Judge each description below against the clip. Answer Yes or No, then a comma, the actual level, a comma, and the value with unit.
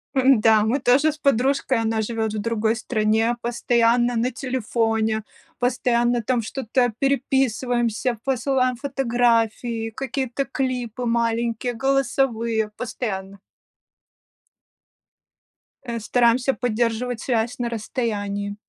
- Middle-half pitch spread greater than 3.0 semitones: No, narrow, 2.4 semitones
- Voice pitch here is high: Yes, high, 235 Hz